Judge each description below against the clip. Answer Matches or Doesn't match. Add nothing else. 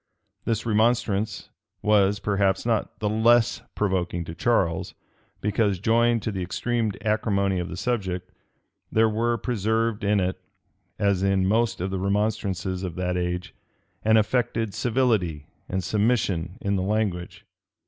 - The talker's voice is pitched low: Matches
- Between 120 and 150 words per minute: Matches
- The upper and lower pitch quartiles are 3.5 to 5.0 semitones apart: Doesn't match